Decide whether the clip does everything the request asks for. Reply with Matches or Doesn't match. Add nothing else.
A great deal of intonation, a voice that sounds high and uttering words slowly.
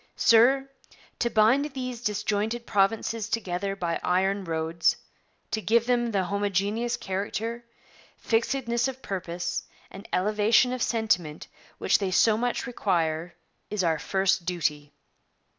Doesn't match